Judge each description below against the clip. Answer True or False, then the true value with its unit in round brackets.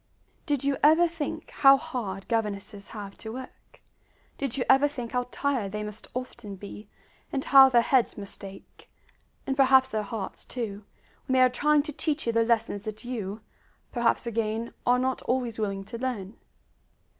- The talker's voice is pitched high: True (235 Hz)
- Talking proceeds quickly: False (175 wpm)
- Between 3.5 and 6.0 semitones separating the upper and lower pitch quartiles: True (3.9 semitones)